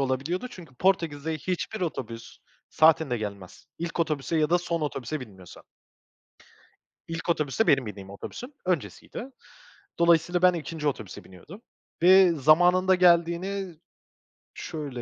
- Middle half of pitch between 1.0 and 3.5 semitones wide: No, average, 4.8 semitones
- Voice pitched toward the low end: No, medium, 165 Hz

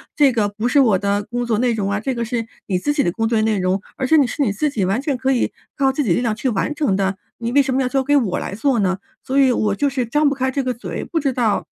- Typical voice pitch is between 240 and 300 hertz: Yes, high, 245 Hz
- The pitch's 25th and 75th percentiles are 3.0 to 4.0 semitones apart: No, average, 4.6 semitones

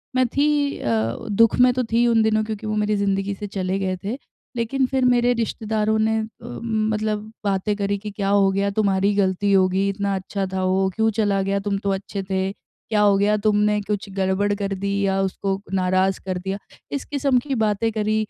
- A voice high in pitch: Yes, high, 205 Hz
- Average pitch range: No, narrow, 2.0 semitones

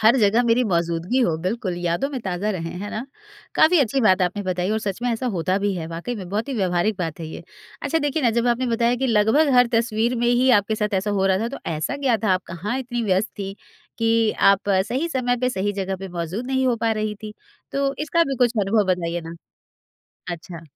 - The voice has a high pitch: Yes, high, 215 Hz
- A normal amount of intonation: Yes, average, 4.7 semitones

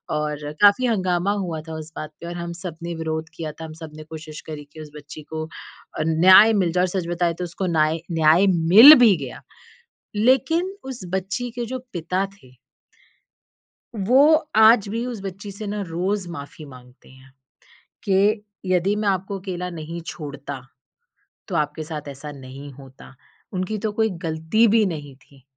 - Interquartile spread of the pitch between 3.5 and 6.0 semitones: Yes, average, 4.6 semitones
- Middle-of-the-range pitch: Yes, medium, 170 Hz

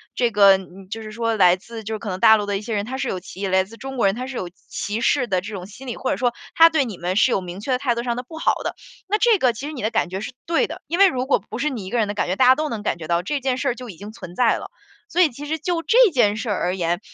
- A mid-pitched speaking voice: No, high, 230 Hz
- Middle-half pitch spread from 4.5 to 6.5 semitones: Yes, average, 5.0 semitones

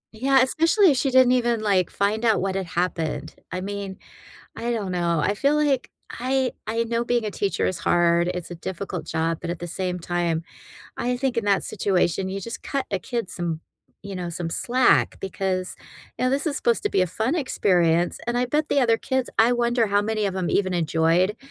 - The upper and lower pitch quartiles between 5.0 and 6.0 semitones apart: Yes, wide, 5.4 semitones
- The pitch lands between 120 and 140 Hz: No, high, 200 Hz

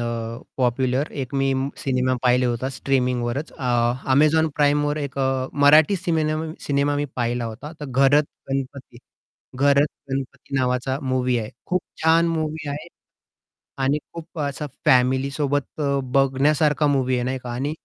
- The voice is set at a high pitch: No, low, 135 Hz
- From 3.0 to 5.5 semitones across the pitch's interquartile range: No, narrow, 2.5 semitones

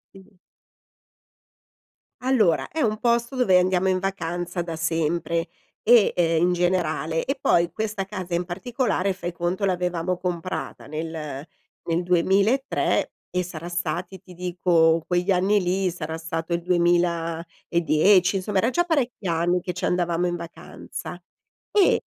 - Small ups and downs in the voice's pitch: Yes, narrow, 2.3 semitones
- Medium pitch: Yes, medium, 180 Hz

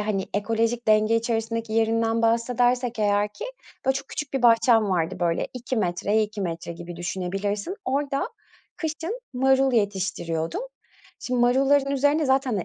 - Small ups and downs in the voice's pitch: No, average, 4.4 semitones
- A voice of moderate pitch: No, high, 230 Hz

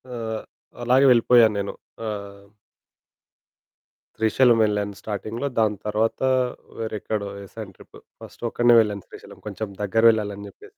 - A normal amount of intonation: No, narrow, 2.0 semitones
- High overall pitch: No, low, 110 Hz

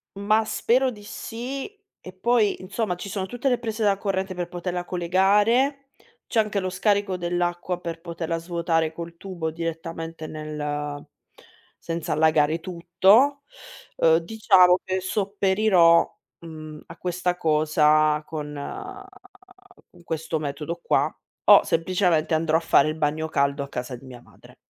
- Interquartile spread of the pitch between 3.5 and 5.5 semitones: Yes, average, 3.9 semitones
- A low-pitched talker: No, medium, 175 Hz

